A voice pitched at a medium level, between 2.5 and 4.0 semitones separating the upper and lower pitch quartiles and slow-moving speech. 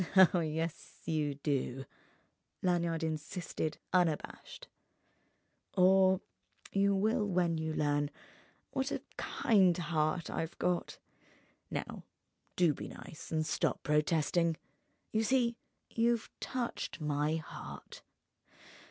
Yes: medium, 165 Hz; average, 3.5 semitones; slow, 100 wpm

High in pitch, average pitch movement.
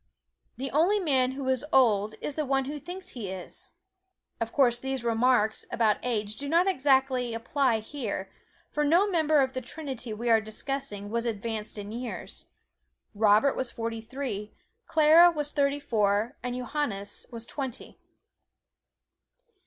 Yes: very high, 255 Hz; average, 4.3 semitones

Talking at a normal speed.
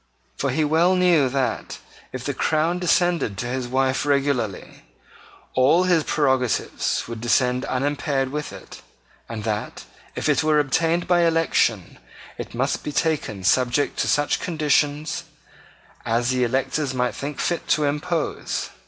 Yes: average, 145 wpm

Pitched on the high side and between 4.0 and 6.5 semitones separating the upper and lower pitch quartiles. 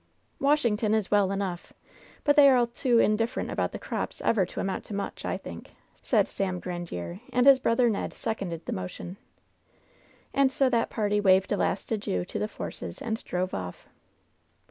Yes: high, 210 Hz; average, 4.4 semitones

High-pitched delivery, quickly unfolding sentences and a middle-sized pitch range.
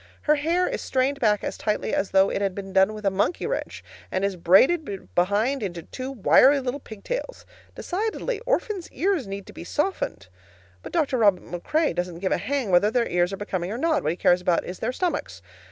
No: high, 210 Hz; fast, 210 wpm; wide, 7.5 semitones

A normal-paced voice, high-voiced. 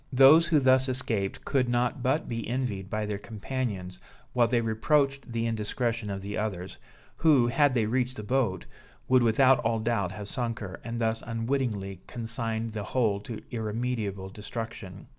No: average, 165 wpm; low, 115 Hz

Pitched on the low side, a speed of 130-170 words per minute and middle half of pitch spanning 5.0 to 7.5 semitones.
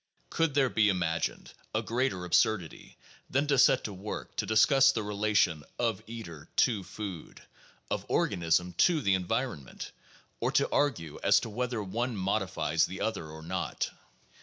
Yes: low, 105 Hz; average, 155 wpm; wide, 5.5 semitones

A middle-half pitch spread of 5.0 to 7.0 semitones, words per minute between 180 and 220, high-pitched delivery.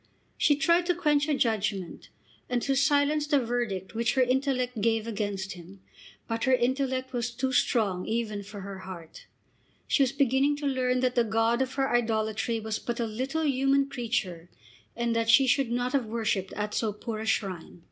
No: average, 3.7 semitones; average, 190 wpm; high, 240 Hz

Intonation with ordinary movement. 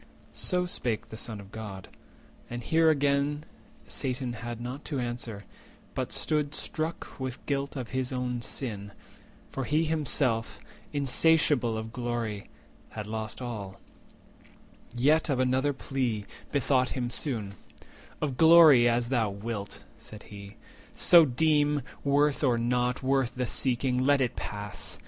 Yes: average, 3.9 semitones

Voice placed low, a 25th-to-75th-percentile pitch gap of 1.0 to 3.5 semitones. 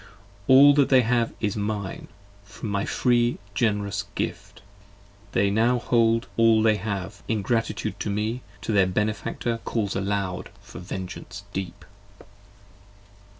Yes: low, 110 Hz; narrow, 2.5 semitones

